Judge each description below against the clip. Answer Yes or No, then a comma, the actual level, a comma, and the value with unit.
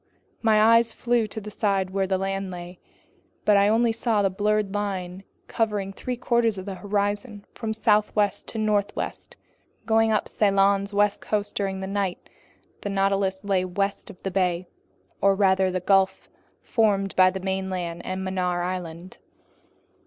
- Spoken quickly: No, average, 155 wpm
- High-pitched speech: Yes, high, 195 Hz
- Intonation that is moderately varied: No, narrow, 1.8 semitones